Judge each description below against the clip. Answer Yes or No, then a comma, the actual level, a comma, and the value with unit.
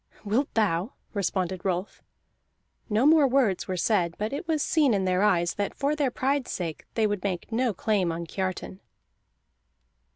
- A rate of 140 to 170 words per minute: Yes, average, 165 wpm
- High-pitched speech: Yes, high, 205 Hz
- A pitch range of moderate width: No, wide, 5.8 semitones